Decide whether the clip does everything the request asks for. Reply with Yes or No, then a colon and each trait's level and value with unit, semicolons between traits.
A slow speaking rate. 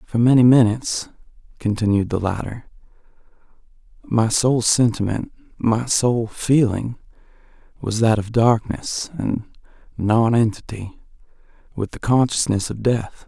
Yes: slow, 95 wpm